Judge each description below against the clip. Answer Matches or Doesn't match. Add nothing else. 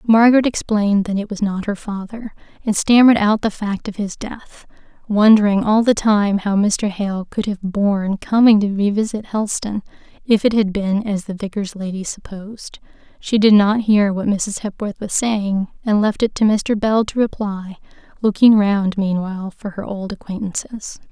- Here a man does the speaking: Doesn't match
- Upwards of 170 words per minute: Matches